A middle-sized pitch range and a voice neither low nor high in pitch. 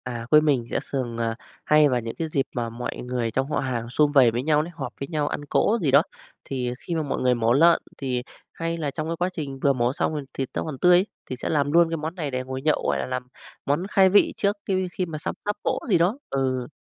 Yes: average, 4.5 semitones; medium, 145 Hz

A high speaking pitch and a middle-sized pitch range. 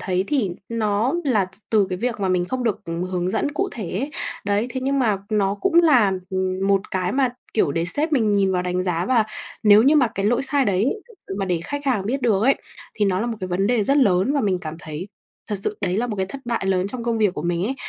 Yes: high, 205 Hz; average, 4.9 semitones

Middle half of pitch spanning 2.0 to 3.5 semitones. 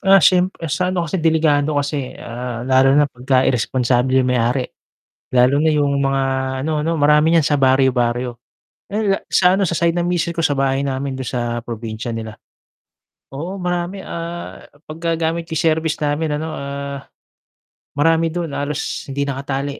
No: average, 4.0 semitones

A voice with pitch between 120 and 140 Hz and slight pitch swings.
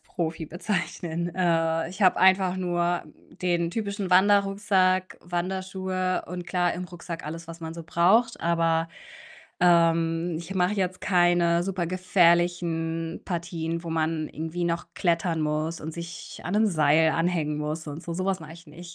No: medium, 175 Hz; narrow, 2.0 semitones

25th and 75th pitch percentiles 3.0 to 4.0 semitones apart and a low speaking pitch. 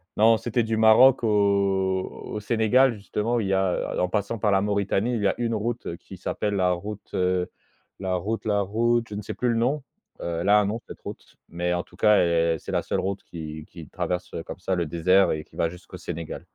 Yes: average, 3.5 semitones; low, 100 Hz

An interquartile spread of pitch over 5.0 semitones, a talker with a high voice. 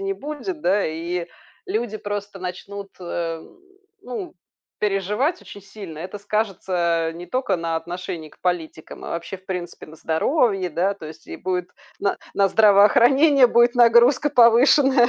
Yes: wide, 5.5 semitones; high, 200 Hz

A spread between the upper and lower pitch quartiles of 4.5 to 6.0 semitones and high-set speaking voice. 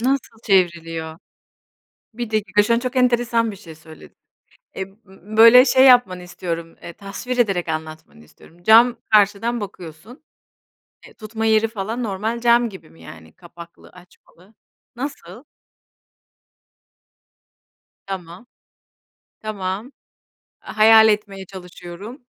Yes: average, 4.9 semitones; high, 205 Hz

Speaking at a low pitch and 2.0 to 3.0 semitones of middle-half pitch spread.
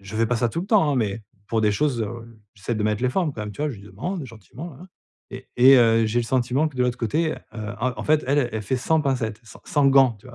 No: low, 125 Hz; average, 4.4 semitones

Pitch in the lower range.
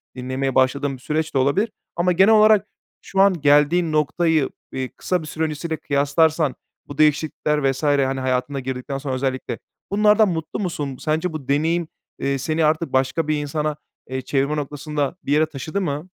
No: medium, 150 Hz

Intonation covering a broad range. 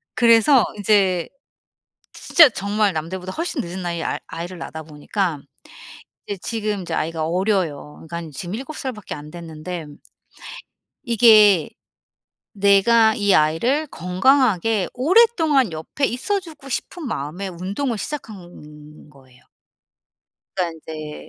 Yes: wide, 6.2 semitones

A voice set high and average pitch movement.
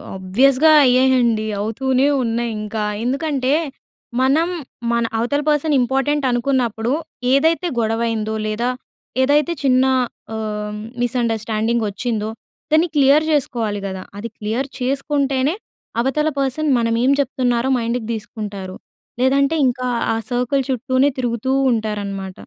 Yes: high, 245 Hz; average, 3.7 semitones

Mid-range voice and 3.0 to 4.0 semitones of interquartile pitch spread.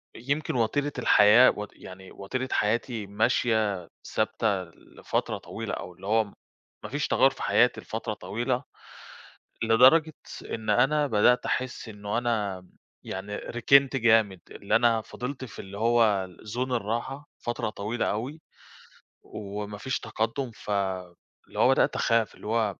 No: low, 115 Hz; average, 3.3 semitones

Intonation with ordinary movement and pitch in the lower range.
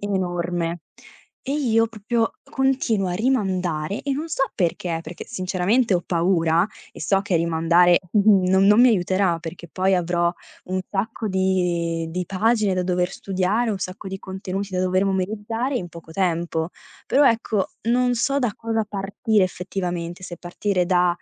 No: average, 3.6 semitones; high, 190 Hz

